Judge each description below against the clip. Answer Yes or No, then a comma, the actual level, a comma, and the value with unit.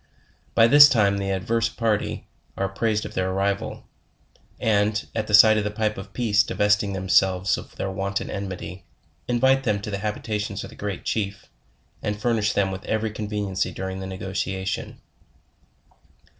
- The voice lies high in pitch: No, low, 100 Hz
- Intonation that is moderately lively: No, narrow, 1.9 semitones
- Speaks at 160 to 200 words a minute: Yes, average, 165 wpm